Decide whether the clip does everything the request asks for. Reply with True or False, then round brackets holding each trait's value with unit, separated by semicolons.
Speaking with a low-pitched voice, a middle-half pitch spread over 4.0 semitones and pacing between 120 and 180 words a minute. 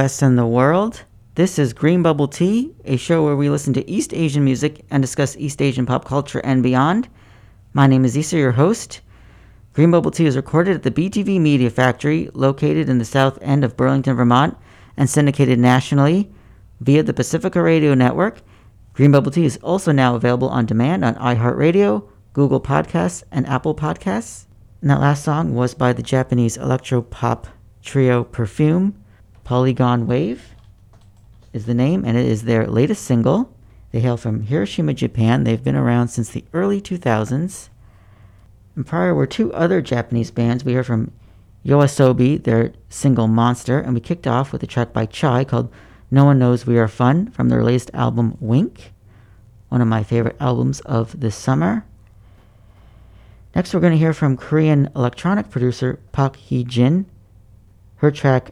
True (125 Hz; 4.4 semitones; 170 wpm)